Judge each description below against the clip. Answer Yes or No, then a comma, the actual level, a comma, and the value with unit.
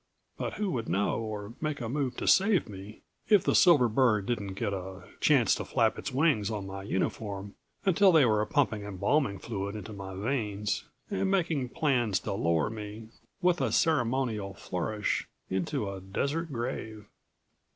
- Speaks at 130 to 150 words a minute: No, average, 165 wpm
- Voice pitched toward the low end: Yes, low, 110 Hz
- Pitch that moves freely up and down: Yes, wide, 5.8 semitones